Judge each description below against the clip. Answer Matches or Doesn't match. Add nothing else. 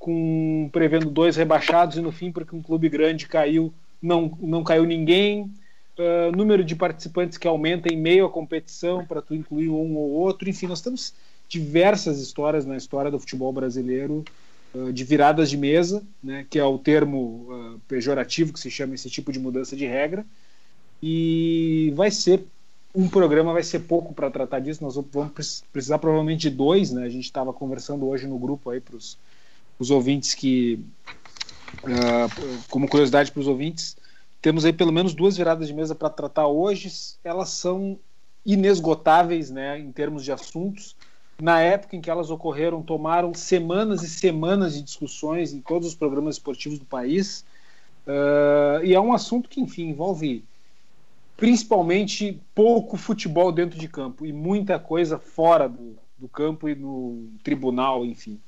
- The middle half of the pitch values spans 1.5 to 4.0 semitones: Matches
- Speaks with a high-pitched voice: Doesn't match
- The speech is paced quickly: Doesn't match